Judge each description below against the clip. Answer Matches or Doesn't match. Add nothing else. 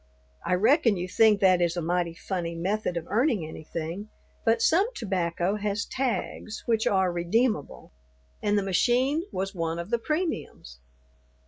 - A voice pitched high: Matches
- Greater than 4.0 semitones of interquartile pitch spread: Matches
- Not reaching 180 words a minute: Matches